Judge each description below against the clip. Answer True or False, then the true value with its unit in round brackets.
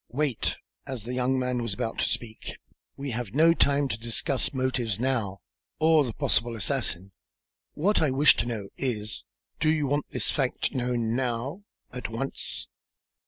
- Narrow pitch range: False (3.5 semitones)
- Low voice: True (125 Hz)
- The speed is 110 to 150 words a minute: False (165 wpm)